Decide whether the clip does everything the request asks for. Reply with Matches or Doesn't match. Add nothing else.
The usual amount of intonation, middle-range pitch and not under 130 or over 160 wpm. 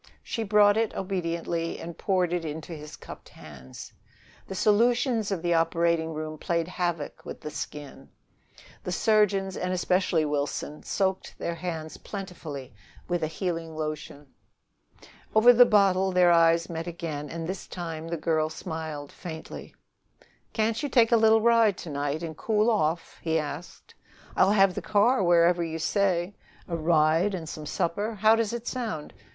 Matches